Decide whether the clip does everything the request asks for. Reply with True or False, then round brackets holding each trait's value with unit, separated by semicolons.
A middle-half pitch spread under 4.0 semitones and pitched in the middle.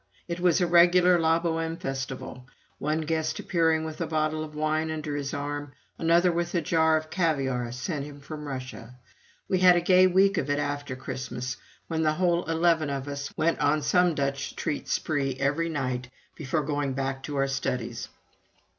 True (3.3 semitones; 155 Hz)